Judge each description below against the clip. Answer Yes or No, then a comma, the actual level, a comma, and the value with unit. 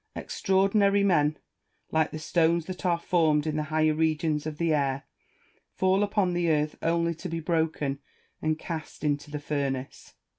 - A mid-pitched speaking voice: Yes, medium, 160 Hz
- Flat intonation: Yes, narrow, 2.3 semitones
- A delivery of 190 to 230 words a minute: No, average, 160 wpm